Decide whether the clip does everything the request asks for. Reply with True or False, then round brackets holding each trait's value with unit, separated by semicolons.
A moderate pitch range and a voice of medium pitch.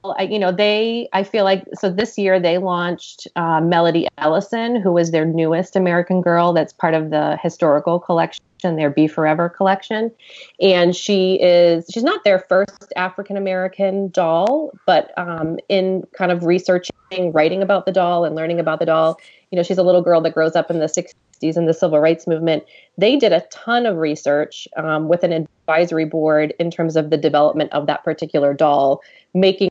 True (3.0 semitones; 175 Hz)